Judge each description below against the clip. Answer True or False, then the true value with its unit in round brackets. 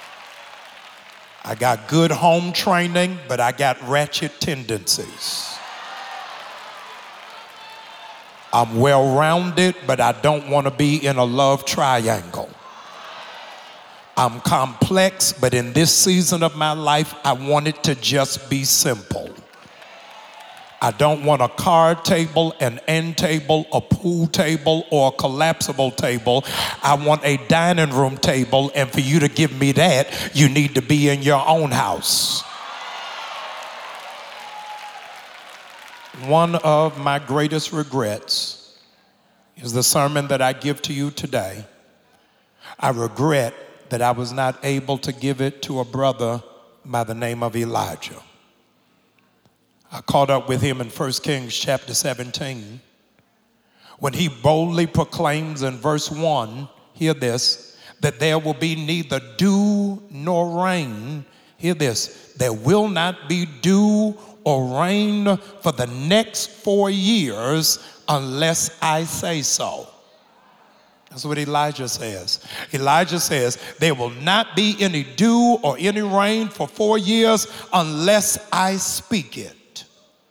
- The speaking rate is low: True (130 wpm)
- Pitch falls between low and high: True (150 Hz)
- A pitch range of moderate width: True (4.2 semitones)